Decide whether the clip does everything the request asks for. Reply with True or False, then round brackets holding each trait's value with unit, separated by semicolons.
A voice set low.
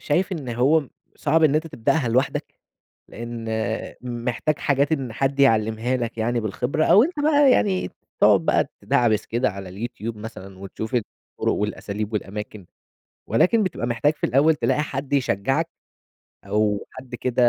True (125 Hz)